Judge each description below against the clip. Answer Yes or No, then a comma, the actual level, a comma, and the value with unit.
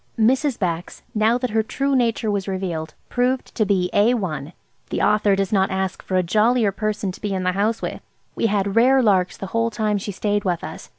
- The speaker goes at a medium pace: No, fast, 215 wpm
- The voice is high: Yes, high, 205 Hz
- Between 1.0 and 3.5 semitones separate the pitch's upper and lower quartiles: Yes, average, 3.2 semitones